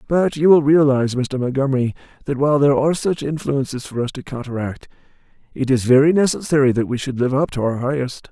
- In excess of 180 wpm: Yes, average, 200 wpm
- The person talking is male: Yes, male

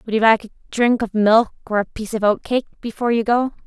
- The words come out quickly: Yes, fast, 245 wpm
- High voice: Yes, high, 225 Hz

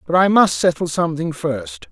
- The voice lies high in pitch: No, medium, 150 Hz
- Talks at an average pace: Yes, average, 190 wpm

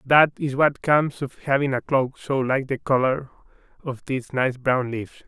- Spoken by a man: Yes, male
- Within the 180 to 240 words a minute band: Yes, average, 195 wpm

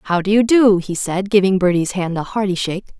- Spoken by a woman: Yes, female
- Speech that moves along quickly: Yes, fast, 240 wpm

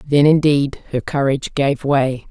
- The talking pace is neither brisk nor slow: Yes, average, 155 wpm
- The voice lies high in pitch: No, medium, 140 Hz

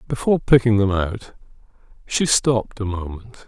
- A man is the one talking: Yes, male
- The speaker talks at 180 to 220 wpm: No, average, 140 wpm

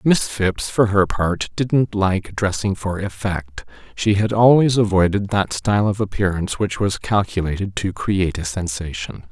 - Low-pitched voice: Yes, low, 100 Hz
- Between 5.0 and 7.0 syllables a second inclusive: No, 4.6 syllables/s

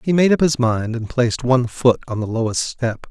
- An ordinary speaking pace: No, fast, 250 wpm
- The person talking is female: No, male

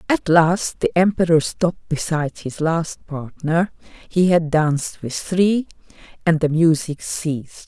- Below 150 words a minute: Yes, average, 140 wpm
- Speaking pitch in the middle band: Yes, medium, 165 Hz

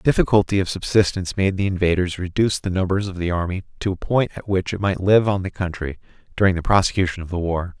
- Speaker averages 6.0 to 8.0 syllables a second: Yes, 6.4 syllables/s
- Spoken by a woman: No, male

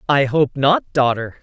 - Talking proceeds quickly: No, average, 170 wpm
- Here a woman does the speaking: Yes, female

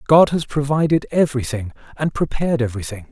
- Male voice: Yes, male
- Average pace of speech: Yes, average, 175 wpm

